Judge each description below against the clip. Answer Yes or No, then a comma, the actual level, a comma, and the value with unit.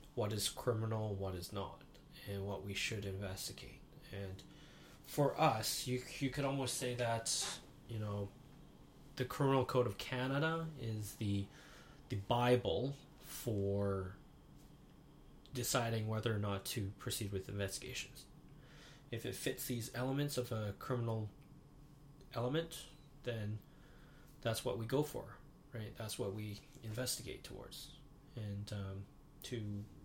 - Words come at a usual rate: No, slow, 130 wpm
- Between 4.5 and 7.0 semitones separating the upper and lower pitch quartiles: Yes, average, 5.3 semitones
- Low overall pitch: Yes, low, 125 Hz